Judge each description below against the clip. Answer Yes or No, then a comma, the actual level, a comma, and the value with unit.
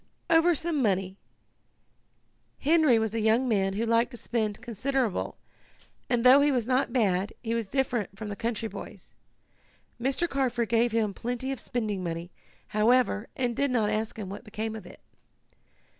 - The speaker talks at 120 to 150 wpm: No, average, 165 wpm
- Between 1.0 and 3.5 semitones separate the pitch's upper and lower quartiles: Yes, average, 3.2 semitones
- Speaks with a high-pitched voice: Yes, high, 230 Hz